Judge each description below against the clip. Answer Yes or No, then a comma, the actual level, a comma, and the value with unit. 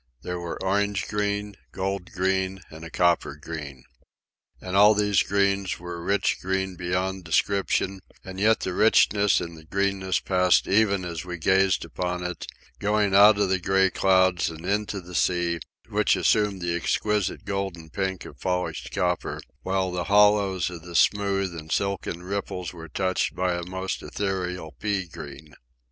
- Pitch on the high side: No, very low, 95 Hz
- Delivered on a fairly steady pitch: Yes, narrow, 2.1 semitones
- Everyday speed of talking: Yes, average, 160 wpm